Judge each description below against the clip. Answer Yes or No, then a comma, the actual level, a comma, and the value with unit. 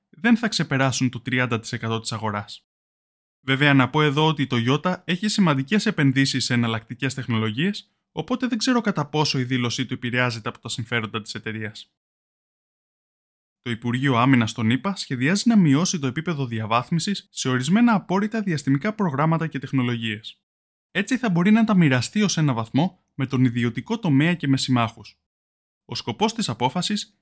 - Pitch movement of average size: No, wide, 7.2 semitones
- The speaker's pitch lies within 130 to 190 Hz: Yes, low, 135 Hz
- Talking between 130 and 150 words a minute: No, average, 160 wpm